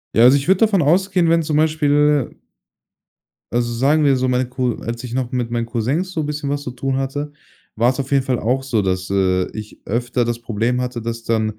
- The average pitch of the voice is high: No, low, 125 Hz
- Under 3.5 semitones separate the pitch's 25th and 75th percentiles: No, average, 3.8 semitones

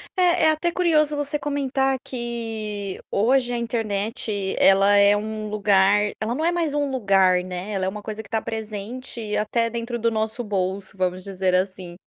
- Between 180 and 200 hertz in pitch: No, high, 220 Hz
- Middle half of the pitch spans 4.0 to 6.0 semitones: Yes, average, 4.3 semitones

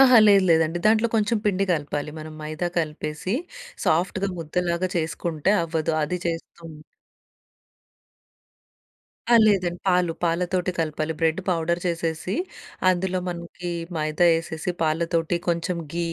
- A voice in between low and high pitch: Yes, medium, 170 Hz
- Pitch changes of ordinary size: No, narrow, 2.2 semitones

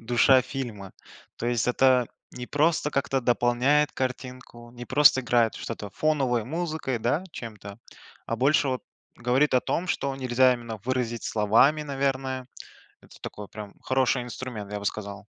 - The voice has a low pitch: Yes, low, 125 Hz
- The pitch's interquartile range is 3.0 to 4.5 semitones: No, narrow, 2.5 semitones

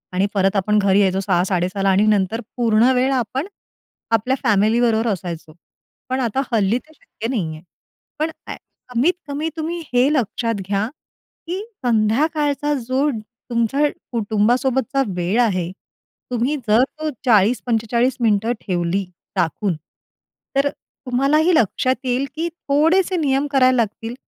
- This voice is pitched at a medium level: No, high, 235 Hz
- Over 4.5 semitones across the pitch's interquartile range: Yes, average, 4.9 semitones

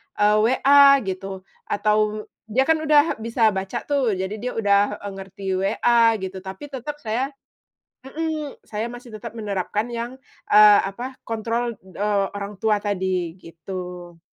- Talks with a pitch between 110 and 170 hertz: No, high, 215 Hz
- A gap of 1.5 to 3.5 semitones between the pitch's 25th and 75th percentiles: No, average, 3.9 semitones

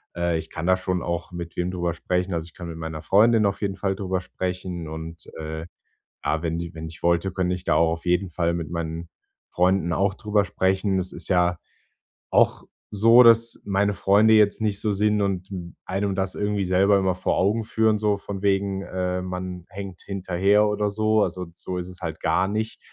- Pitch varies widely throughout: No, narrow, 2.6 semitones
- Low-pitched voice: Yes, very low, 95 Hz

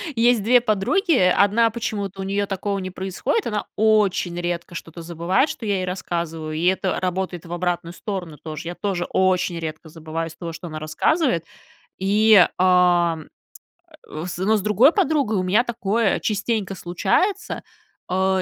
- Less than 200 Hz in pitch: Yes, high, 190 Hz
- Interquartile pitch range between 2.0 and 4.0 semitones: Yes, average, 3.6 semitones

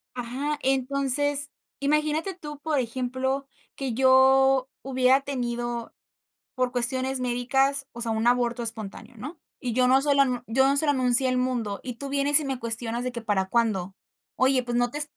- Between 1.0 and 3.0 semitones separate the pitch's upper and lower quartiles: Yes, narrow, 2.4 semitones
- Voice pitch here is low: No, very high, 255 Hz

